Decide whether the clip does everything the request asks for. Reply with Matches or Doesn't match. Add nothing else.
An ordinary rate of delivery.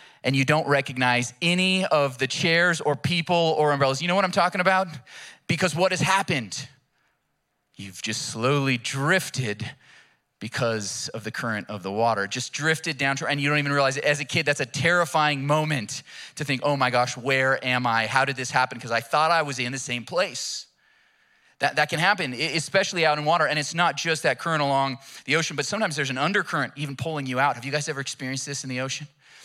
Doesn't match